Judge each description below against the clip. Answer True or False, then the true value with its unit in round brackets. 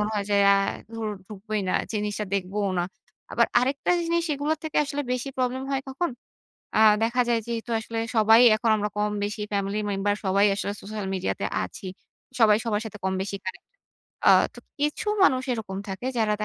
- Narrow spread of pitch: False (3.7 semitones)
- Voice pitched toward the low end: False (215 Hz)